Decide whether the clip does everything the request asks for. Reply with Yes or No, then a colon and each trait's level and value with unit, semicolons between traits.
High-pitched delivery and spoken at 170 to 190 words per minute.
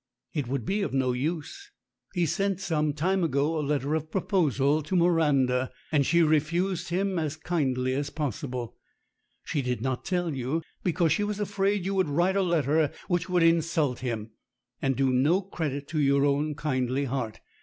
No: medium, 155 Hz; average, 180 wpm